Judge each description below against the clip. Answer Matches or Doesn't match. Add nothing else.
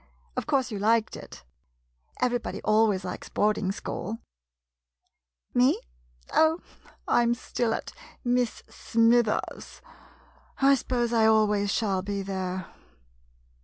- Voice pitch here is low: Doesn't match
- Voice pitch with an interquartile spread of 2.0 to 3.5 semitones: Matches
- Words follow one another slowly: Matches